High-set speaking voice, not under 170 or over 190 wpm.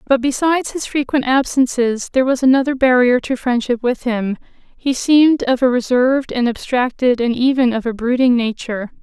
Yes: very high, 255 Hz; average, 175 wpm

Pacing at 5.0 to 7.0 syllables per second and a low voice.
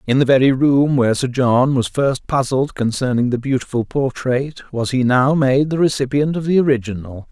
Yes: 5.1 syllables/s; low, 130 Hz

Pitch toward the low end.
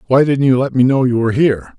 Yes: low, 130 Hz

